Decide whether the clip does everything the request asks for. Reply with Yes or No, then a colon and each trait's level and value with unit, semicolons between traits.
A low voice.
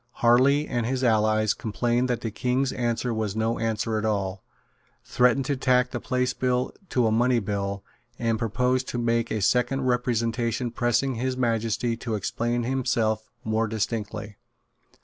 Yes: low, 120 Hz